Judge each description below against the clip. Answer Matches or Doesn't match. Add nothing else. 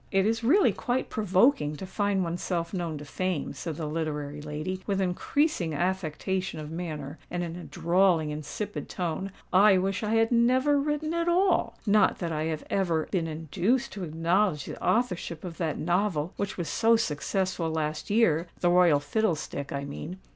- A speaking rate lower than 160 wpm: Doesn't match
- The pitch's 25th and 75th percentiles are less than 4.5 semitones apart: Doesn't match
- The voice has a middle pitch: Matches